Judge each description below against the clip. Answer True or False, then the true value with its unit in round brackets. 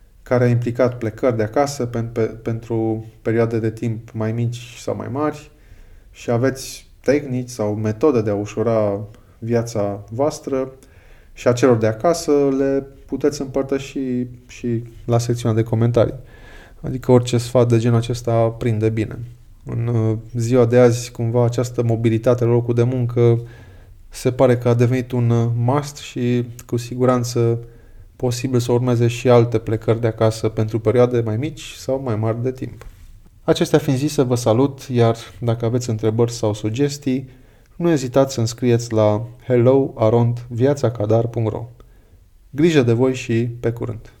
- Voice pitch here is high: False (120 Hz)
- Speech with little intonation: True (2.2 semitones)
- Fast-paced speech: False (150 wpm)